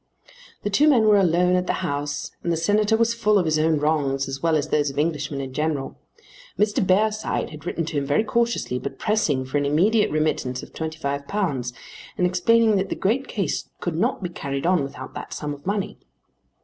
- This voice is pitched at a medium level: Yes, medium, 165 Hz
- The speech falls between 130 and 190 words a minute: No, fast, 205 wpm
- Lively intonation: Yes, wide, 6.2 semitones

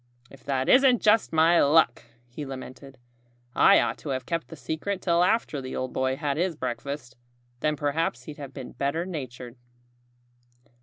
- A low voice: No, medium, 145 Hz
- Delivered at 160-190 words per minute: Yes, average, 165 wpm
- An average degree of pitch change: Yes, average, 4.1 semitones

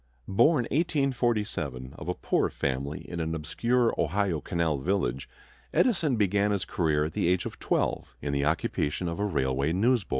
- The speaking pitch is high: No, very low, 90 Hz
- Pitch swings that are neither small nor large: No, wide, 7.1 semitones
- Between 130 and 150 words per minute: No, average, 165 wpm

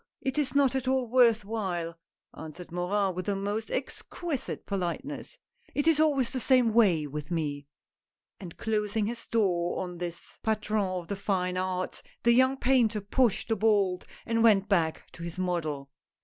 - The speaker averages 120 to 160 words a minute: No, average, 170 wpm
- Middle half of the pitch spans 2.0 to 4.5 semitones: No, average, 5.0 semitones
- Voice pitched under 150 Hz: No, high, 205 Hz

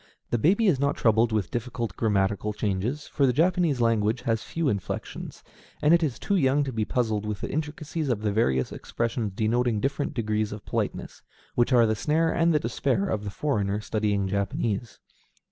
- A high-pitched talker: No, low, 115 Hz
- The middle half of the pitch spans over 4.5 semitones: Yes, average, 5.1 semitones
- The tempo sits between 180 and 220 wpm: Yes, average, 185 wpm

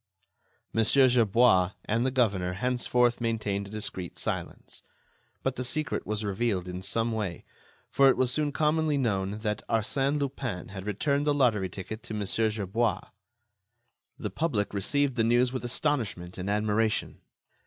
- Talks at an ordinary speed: Yes, average, 150 wpm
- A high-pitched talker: No, low, 115 Hz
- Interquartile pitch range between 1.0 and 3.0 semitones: No, average, 4.3 semitones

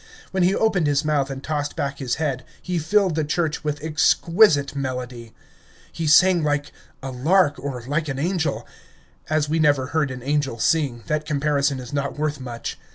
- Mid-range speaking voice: Yes, medium, 145 Hz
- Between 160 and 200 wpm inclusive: Yes, average, 180 wpm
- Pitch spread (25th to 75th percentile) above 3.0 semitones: No, average, 2.7 semitones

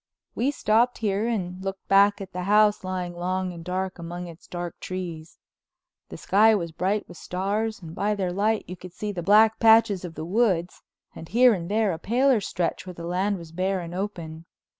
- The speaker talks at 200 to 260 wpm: Yes, fast, 205 wpm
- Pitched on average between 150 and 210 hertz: Yes, high, 190 Hz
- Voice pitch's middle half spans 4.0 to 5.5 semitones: No, average, 3.2 semitones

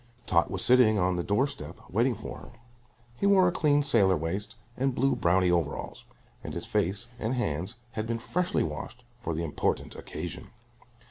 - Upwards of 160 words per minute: Yes, average, 180 wpm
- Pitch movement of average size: No, wide, 6.3 semitones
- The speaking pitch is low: Yes, low, 110 Hz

